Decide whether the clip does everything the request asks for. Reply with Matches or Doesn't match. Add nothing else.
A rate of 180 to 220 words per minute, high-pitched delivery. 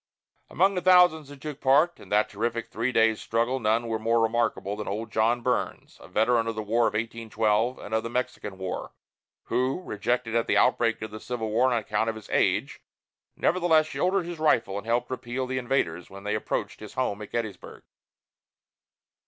Doesn't match